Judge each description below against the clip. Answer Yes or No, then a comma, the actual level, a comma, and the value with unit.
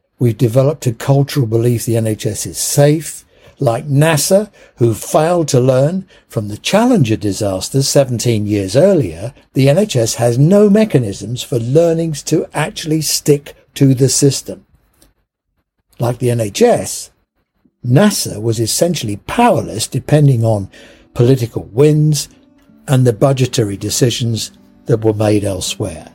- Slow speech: Yes, slow, 125 wpm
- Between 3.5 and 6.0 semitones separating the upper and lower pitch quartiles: Yes, average, 4.6 semitones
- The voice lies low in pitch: Yes, low, 130 Hz